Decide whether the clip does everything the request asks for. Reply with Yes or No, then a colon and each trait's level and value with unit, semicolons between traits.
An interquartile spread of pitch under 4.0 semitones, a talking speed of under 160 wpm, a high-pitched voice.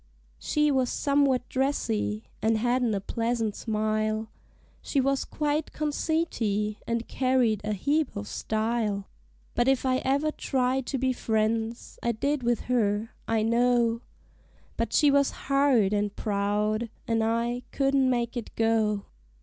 Yes: average, 3.5 semitones; average, 140 wpm; high, 235 Hz